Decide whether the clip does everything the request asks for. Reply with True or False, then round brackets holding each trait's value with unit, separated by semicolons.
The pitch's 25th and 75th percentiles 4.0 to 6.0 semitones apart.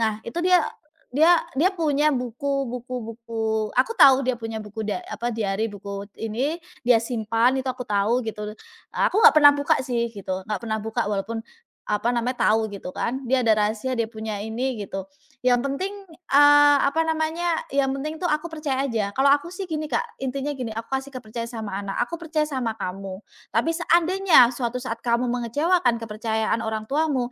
True (4.8 semitones)